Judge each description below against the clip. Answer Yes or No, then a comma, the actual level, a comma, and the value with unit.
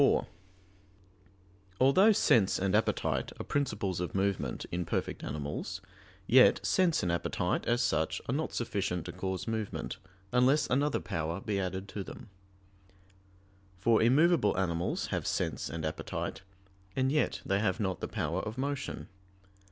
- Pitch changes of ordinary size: No, wide, 6.2 semitones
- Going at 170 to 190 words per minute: No, average, 145 wpm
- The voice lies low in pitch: Yes, low, 100 Hz